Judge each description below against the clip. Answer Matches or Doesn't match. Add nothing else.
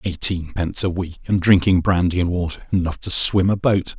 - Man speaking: Matches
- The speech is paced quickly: Doesn't match